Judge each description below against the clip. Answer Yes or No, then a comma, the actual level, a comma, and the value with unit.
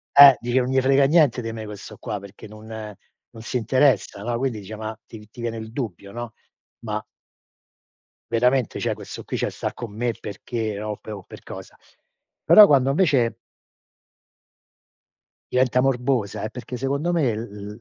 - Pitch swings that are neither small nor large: Yes, average, 3.4 semitones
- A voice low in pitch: Yes, low, 120 Hz